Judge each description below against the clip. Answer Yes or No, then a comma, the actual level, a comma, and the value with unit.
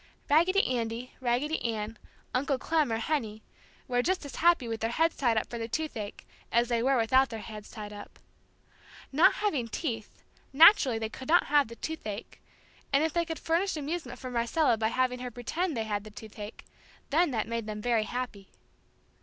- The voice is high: Yes, high, 245 Hz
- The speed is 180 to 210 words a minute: Yes, average, 185 wpm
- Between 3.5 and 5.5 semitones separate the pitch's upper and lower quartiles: Yes, average, 5.2 semitones